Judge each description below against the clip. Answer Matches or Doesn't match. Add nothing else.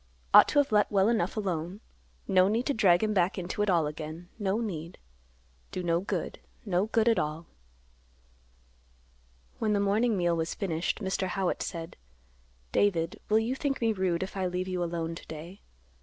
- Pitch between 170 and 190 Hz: Matches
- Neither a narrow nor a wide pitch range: Matches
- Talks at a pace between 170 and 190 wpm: Matches